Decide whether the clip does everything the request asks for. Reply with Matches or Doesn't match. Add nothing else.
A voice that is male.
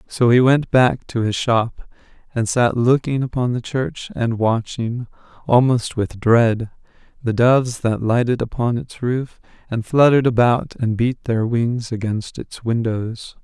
Matches